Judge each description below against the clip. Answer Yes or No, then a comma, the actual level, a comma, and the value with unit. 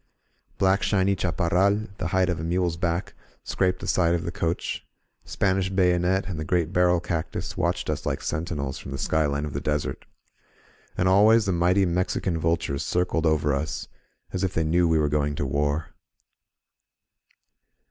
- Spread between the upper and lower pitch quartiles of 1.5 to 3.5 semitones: Yes, average, 3.1 semitones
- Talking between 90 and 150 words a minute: No, average, 175 wpm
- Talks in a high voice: No, very low, 85 Hz